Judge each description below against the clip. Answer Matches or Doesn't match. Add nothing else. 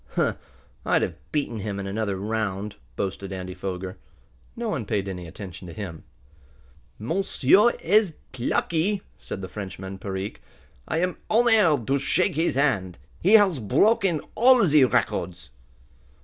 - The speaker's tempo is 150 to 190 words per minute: Doesn't match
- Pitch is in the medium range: Doesn't match